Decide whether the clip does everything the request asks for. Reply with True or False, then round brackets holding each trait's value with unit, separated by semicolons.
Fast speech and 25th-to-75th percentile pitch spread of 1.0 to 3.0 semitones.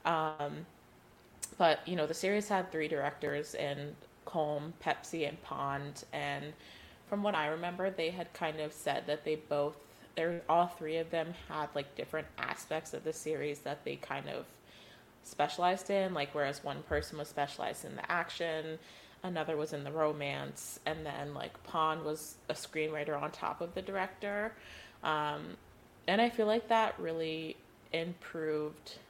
False (165 wpm; 2.6 semitones)